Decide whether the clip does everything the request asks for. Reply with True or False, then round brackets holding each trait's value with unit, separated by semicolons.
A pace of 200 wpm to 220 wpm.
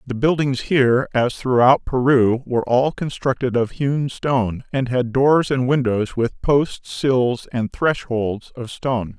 False (155 wpm)